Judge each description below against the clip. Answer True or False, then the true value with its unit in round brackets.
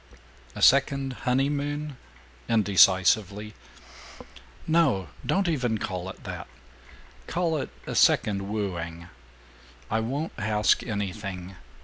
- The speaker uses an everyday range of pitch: False (6.2 semitones)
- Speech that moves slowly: True (95 wpm)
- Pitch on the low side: True (110 Hz)